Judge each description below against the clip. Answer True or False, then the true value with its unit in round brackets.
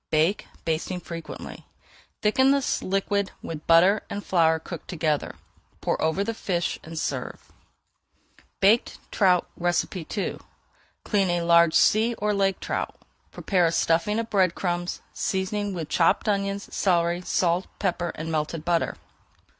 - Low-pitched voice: False (180 Hz)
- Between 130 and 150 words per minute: True (140 wpm)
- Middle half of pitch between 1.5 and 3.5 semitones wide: True (3.2 semitones)